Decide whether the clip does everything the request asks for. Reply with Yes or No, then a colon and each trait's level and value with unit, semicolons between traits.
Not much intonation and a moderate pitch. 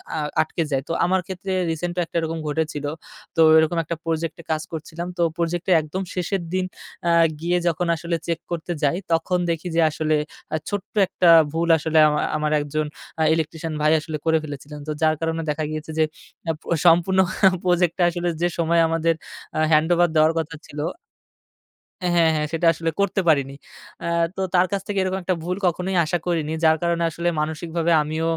Yes: narrow, 1.9 semitones; medium, 165 Hz